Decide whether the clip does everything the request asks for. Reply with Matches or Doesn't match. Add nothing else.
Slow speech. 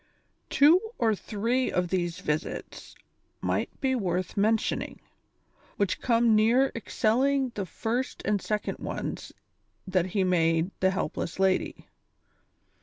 Matches